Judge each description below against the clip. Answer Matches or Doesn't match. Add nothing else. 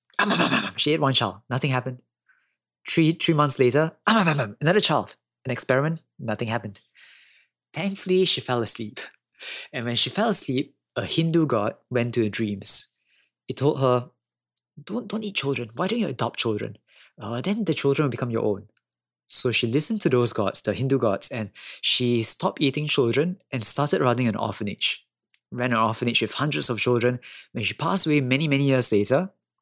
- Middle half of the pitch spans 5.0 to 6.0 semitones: Matches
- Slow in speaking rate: Doesn't match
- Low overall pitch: Matches